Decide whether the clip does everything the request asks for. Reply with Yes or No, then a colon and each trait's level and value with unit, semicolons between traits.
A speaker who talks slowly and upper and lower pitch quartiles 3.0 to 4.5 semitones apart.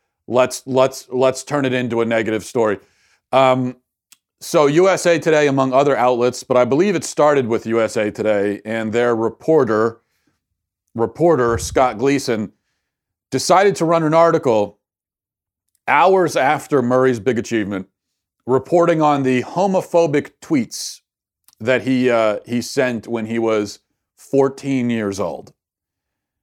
Yes: slow, 125 wpm; average, 4.0 semitones